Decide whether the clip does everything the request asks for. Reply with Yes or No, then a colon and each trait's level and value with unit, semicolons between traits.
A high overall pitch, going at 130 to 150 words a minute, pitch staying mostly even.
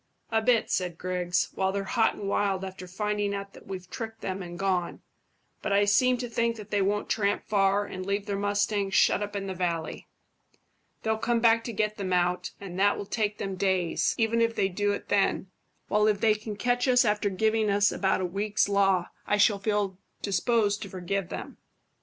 No: high, 200 Hz; fast, 205 wpm; narrow, 2.0 semitones